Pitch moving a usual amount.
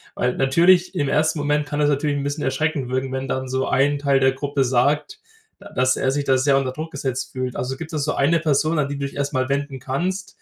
No: narrow, 2.1 semitones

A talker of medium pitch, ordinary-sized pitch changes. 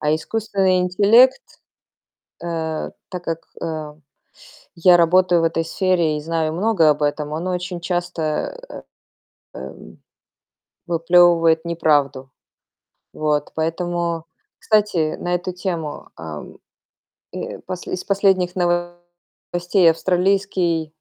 No: medium, 175 Hz; narrow, 2.2 semitones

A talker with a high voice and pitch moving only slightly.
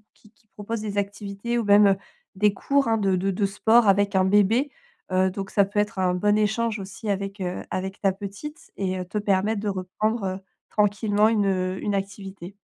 Yes: high, 200 Hz; narrow, 1.8 semitones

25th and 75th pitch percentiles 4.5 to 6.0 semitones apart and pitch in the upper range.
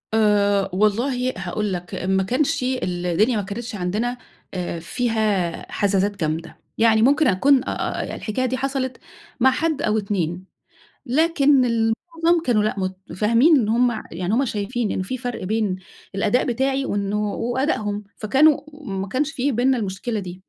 Yes: average, 4.8 semitones; high, 220 Hz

